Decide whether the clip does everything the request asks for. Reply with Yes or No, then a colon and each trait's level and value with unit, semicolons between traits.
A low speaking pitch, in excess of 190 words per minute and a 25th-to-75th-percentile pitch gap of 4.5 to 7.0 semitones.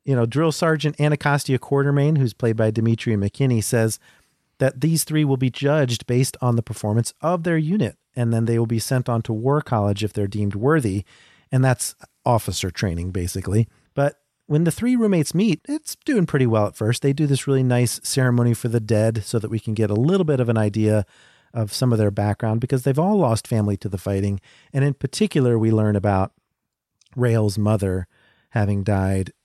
Yes: low, 120 Hz; average, 200 wpm; average, 4.9 semitones